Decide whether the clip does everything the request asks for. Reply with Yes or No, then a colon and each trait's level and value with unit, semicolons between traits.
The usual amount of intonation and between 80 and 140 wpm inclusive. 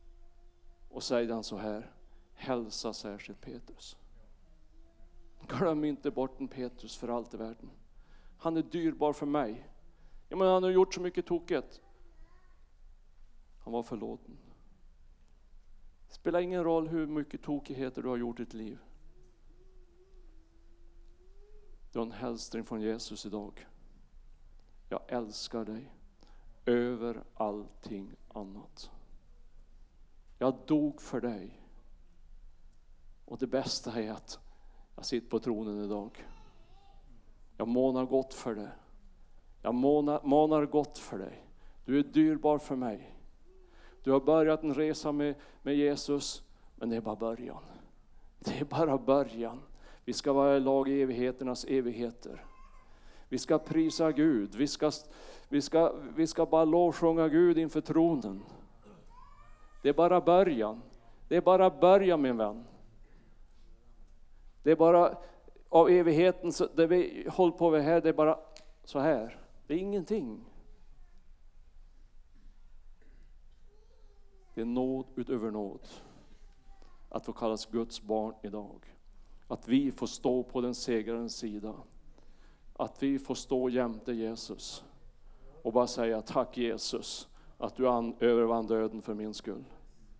No: wide, 6.0 semitones; average, 130 wpm